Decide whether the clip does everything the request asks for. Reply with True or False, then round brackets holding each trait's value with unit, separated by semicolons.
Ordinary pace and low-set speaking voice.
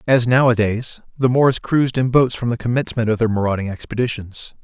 True (180 wpm; 120 Hz)